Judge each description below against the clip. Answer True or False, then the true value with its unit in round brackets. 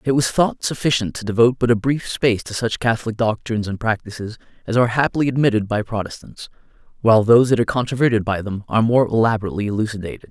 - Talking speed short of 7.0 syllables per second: False (7.1 syllables/s)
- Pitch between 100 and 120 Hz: True (115 Hz)